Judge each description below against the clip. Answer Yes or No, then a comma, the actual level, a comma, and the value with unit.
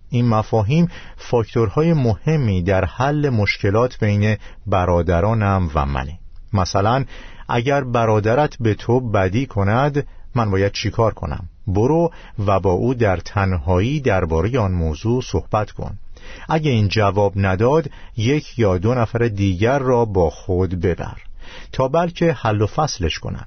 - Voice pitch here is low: Yes, low, 110 Hz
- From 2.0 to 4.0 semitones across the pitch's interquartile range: No, average, 4.8 semitones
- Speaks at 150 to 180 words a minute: No, average, 135 wpm